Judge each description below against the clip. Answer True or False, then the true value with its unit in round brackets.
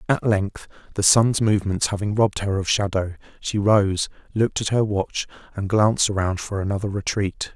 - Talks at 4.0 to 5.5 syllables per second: True (5.2 syllables/s)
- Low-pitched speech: True (100 Hz)